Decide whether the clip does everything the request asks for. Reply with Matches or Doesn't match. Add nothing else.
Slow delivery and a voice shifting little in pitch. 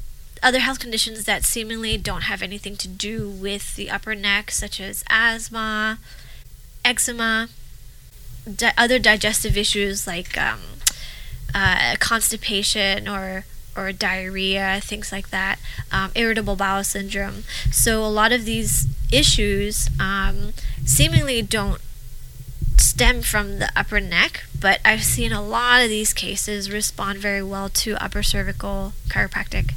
Matches